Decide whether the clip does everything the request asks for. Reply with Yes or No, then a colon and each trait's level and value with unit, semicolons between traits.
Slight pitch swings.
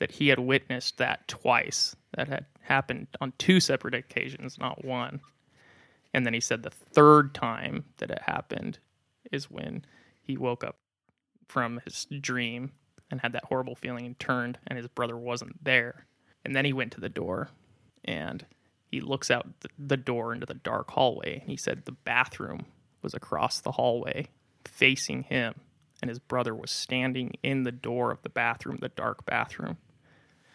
Yes: narrow, 1.9 semitones